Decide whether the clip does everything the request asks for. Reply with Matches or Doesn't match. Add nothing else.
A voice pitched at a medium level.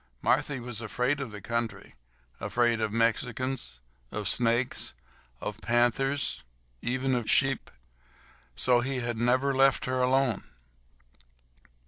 Doesn't match